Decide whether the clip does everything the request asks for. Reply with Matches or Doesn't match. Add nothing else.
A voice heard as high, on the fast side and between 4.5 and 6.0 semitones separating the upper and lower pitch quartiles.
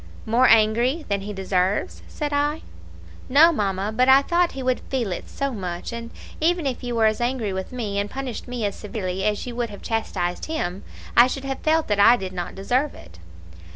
Matches